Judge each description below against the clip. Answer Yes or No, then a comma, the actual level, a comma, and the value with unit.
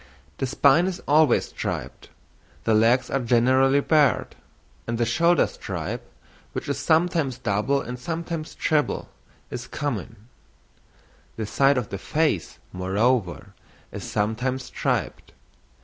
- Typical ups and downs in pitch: Yes, average, 4.8 semitones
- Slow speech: Yes, slow, 120 wpm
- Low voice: Yes, low, 130 Hz